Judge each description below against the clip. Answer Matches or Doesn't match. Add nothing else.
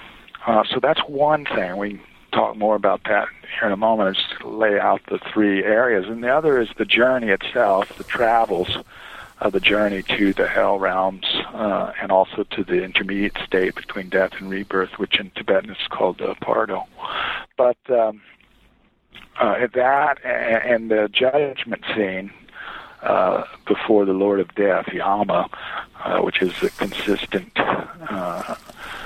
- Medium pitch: Doesn't match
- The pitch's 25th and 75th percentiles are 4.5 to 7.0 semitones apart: Doesn't match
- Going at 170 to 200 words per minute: Doesn't match